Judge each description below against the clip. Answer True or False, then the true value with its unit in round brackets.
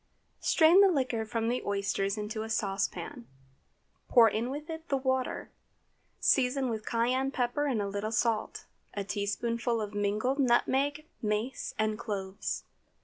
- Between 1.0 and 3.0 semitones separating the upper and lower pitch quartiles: False (3.8 semitones)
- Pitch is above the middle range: True (230 Hz)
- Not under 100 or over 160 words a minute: True (145 wpm)